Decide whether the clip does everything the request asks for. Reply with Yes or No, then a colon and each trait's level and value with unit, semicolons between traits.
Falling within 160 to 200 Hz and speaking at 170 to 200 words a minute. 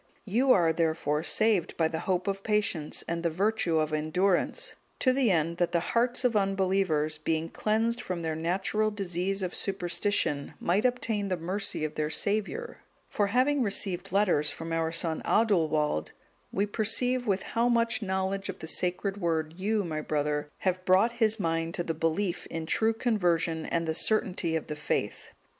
Yes: medium, 185 Hz; average, 175 wpm